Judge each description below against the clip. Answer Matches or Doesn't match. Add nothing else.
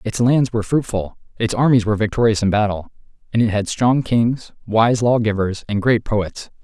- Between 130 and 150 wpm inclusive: Doesn't match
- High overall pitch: Doesn't match